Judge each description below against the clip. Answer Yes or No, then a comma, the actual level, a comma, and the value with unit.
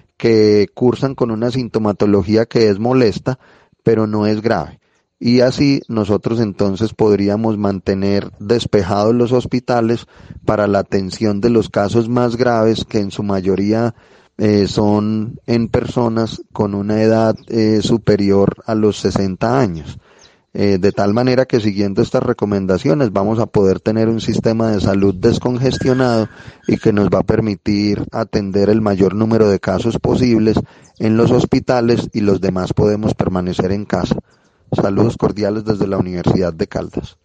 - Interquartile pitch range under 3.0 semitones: Yes, narrow, 2.6 semitones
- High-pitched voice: No, low, 110 Hz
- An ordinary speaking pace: Yes, average, 150 wpm